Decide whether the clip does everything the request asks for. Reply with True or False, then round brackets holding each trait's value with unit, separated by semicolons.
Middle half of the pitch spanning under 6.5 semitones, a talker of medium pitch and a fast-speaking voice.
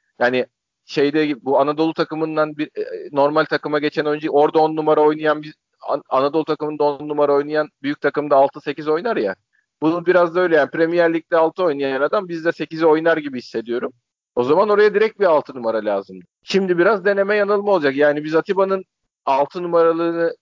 True (2.7 semitones; 155 Hz; 175 wpm)